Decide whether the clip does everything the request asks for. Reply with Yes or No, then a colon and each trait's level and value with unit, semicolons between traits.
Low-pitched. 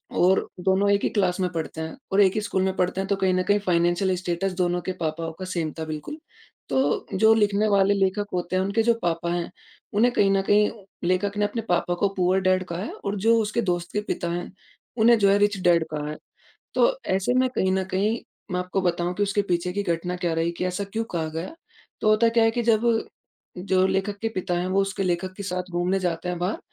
No: high, 190 Hz